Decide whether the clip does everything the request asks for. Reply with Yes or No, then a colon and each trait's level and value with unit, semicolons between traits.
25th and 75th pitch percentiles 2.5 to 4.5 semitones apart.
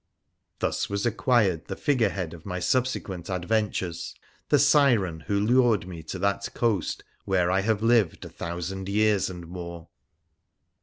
Yes: average, 4.1 semitones